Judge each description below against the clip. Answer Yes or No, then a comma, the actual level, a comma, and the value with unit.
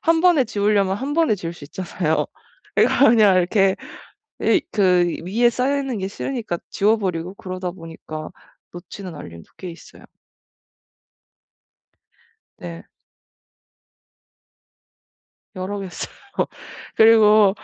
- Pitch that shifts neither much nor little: Yes, average, 4.2 semitones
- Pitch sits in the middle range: No, high, 195 Hz